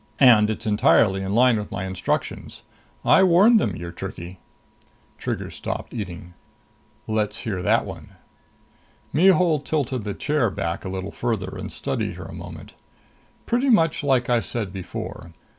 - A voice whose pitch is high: No, low, 110 Hz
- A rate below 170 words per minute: Yes, average, 150 wpm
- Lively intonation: Yes, wide, 7.2 semitones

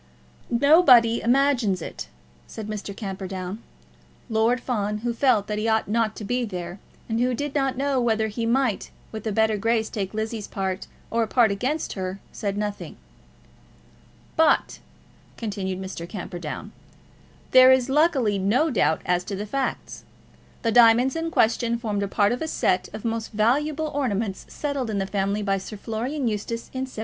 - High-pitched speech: Yes, high, 225 Hz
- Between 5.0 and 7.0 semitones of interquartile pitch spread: No, average, 3.8 semitones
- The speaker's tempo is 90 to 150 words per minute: No, average, 170 wpm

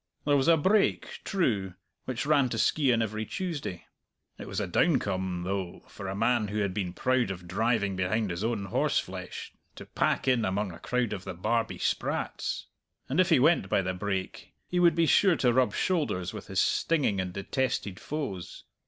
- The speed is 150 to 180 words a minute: No, average, 190 wpm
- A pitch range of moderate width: No, wide, 6.6 semitones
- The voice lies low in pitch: Yes, low, 110 Hz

